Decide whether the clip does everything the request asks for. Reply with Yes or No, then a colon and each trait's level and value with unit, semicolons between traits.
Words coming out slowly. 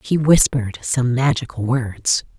Yes: slow, 125 wpm